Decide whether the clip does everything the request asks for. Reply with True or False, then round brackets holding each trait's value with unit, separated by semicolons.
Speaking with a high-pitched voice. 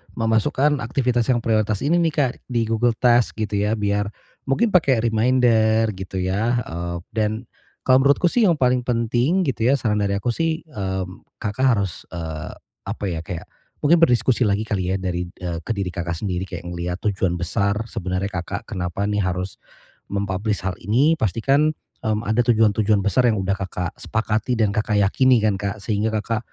False (110 Hz)